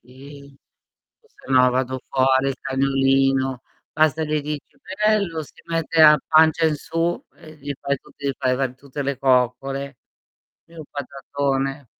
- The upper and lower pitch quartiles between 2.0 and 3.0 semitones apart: Yes, narrow, 2.4 semitones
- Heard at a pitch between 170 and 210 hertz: No, medium, 140 Hz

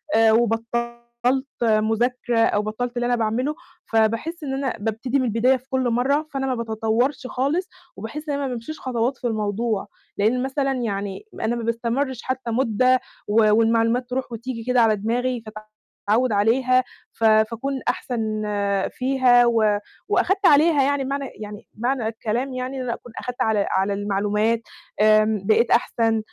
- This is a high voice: Yes, high, 235 Hz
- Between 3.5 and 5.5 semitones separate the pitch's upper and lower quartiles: No, average, 2.8 semitones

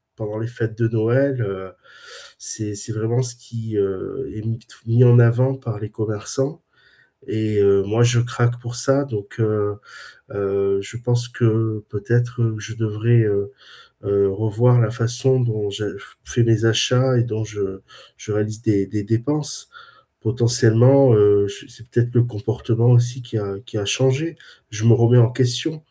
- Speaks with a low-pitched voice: Yes, low, 115 Hz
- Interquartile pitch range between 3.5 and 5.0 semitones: No, narrow, 2.4 semitones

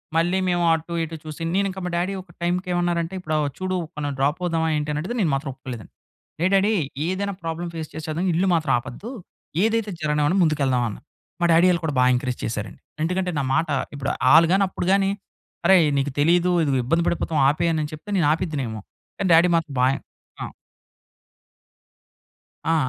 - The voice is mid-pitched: Yes, medium, 165 Hz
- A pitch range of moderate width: Yes, average, 3.3 semitones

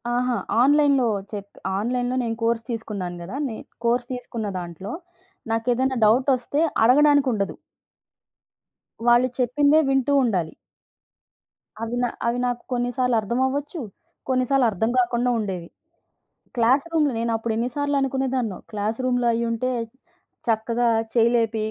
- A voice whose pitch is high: Yes, high, 240 Hz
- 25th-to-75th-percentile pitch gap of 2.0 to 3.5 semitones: Yes, narrow, 2.6 semitones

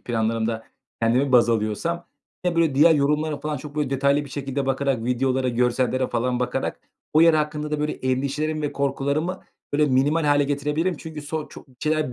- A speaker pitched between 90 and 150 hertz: Yes, medium, 140 Hz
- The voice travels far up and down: No, average, 2.9 semitones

